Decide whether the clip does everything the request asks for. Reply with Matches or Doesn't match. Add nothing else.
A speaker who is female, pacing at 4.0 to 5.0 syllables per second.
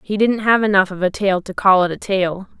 Doesn't match